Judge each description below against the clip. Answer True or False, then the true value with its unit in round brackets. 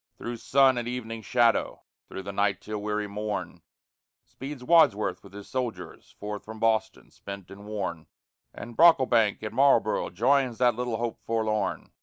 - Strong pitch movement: False (3.0 semitones)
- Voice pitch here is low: True (110 Hz)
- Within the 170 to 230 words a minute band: False (155 wpm)